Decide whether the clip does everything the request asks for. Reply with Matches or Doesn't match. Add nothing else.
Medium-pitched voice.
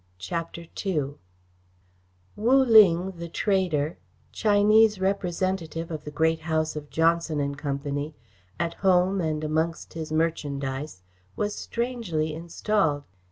Matches